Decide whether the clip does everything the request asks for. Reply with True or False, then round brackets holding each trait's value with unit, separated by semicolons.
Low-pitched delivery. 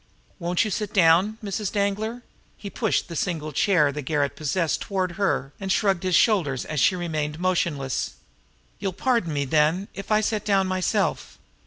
False (185 Hz)